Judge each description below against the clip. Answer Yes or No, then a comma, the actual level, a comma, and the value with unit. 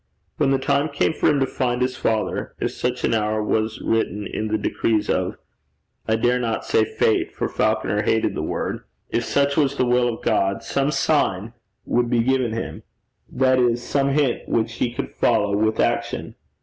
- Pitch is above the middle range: No, low, 120 Hz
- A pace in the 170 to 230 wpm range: Yes, average, 190 wpm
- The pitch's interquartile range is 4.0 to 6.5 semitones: No, average, 3.2 semitones